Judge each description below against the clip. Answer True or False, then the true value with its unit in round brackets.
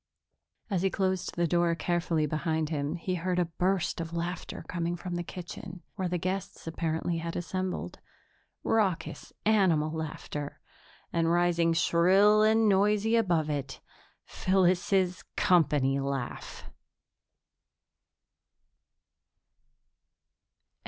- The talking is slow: True (105 wpm)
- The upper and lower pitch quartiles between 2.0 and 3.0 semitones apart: True (2.4 semitones)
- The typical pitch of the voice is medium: True (175 Hz)